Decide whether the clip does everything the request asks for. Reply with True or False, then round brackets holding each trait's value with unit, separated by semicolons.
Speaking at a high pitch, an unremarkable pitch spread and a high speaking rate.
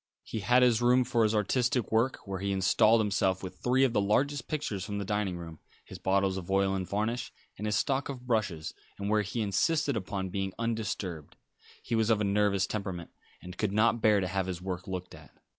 False (105 Hz; 3.4 semitones; 215 wpm)